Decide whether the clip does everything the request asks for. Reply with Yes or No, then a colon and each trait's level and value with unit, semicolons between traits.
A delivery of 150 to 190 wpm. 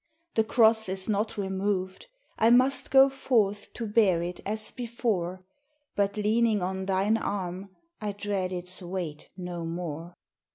No: average, 140 wpm